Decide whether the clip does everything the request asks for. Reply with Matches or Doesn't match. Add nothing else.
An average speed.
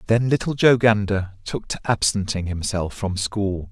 Matches